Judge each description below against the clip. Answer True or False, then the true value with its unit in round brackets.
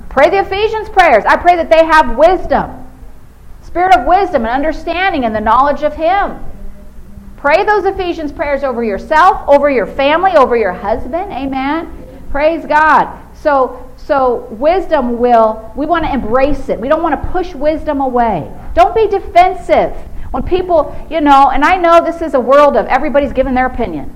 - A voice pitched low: False (305 Hz)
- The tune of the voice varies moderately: True (4.5 semitones)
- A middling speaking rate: True (175 wpm)